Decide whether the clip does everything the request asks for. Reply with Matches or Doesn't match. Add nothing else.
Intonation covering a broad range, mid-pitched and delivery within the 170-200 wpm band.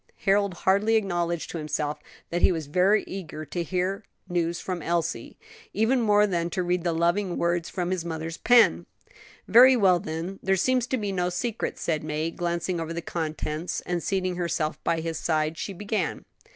Doesn't match